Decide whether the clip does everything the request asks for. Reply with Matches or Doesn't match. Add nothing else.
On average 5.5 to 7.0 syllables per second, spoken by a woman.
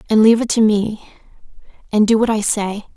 Matches